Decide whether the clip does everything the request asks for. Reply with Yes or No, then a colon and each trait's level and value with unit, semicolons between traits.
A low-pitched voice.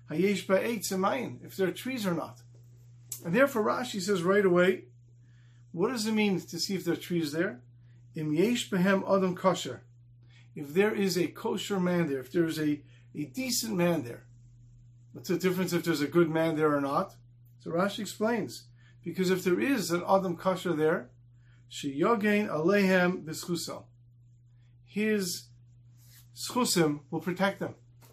No: medium, 170 Hz